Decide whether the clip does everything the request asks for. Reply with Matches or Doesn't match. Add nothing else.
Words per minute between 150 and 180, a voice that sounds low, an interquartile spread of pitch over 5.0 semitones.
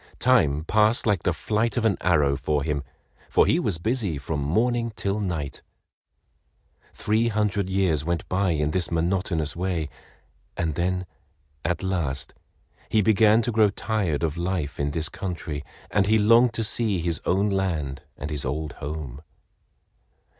Matches